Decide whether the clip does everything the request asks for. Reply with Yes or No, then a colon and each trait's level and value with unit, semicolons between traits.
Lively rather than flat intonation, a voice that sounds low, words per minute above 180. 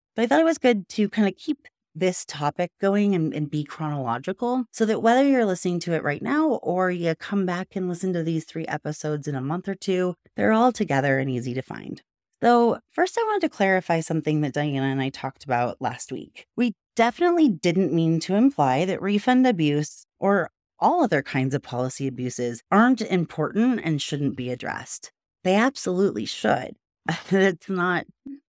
No: wide, 6.6 semitones; medium, 180 Hz; average, 190 wpm